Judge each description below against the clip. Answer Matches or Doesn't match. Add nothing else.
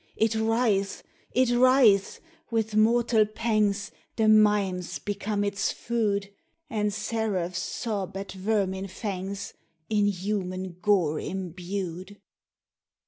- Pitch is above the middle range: Matches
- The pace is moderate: Doesn't match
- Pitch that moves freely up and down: Doesn't match